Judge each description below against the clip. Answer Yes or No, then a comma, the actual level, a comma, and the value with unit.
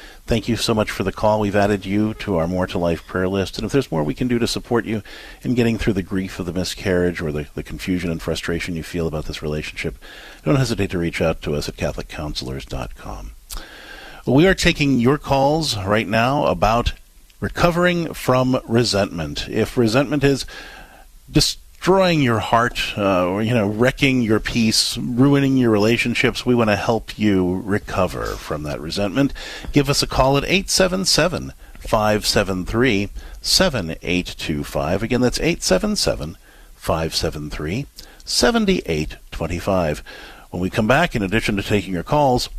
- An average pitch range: No, wide, 6.2 semitones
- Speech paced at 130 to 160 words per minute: Yes, average, 155 wpm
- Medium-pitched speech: No, low, 105 Hz